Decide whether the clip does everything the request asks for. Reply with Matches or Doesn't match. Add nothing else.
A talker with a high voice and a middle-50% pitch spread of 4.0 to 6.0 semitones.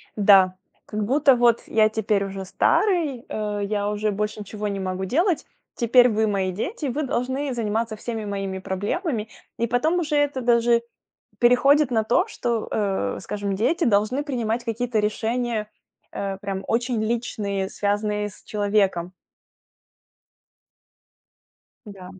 Doesn't match